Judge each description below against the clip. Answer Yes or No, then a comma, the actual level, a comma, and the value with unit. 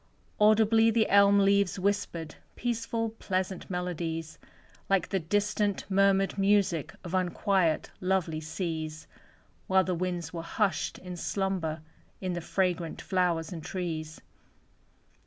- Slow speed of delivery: Yes, slow, 120 wpm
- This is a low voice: No, medium, 185 Hz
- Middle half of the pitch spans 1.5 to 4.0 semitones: Yes, average, 3.1 semitones